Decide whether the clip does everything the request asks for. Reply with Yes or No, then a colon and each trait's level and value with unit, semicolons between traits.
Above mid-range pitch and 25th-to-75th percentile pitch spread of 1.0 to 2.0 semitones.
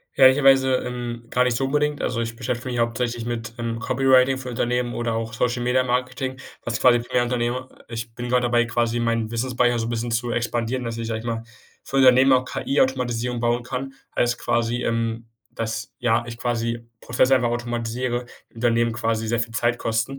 No: low, 120 Hz; narrow, 1.5 semitones